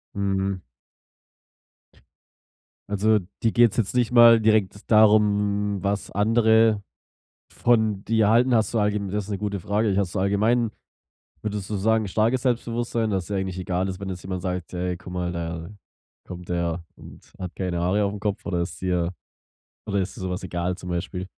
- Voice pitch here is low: Yes, low, 100 Hz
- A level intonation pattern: No, average, 3.1 semitones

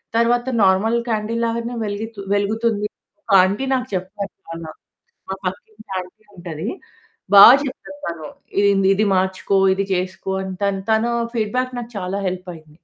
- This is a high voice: Yes, high, 200 Hz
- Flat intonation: No, average, 3.5 semitones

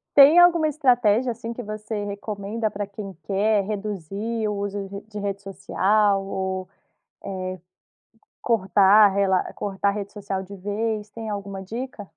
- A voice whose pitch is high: Yes, high, 205 Hz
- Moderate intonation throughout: No, narrow, 1.9 semitones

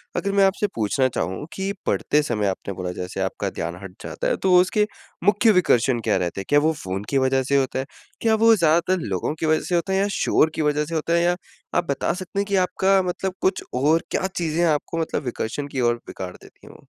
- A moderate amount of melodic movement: No, wide, 7.7 semitones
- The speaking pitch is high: No, medium, 155 Hz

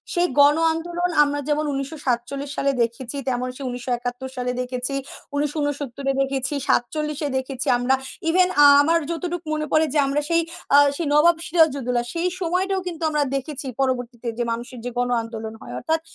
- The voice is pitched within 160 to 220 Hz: No, very high, 280 Hz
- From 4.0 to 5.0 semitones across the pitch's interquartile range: Yes, average, 4.3 semitones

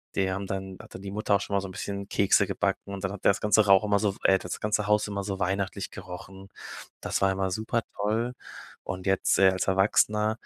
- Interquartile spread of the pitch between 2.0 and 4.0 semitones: No, narrow, 1.4 semitones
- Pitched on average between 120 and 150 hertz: No, low, 100 Hz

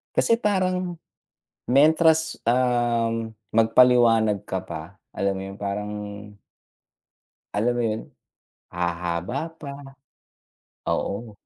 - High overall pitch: No, low, 115 Hz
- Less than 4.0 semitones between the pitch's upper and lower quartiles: No, wide, 5.6 semitones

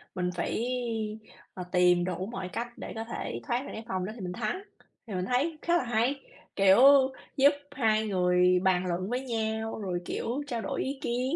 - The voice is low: No, high, 220 Hz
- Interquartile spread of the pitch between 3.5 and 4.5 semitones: No, average, 5.2 semitones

